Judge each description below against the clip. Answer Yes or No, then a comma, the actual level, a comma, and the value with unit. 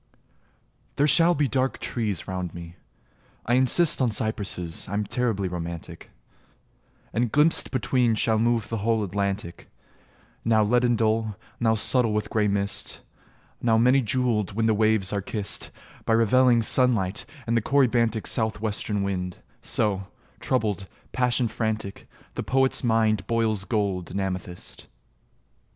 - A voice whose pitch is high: No, low, 110 Hz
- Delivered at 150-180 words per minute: No, slow, 135 wpm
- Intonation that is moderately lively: Yes, average, 3.2 semitones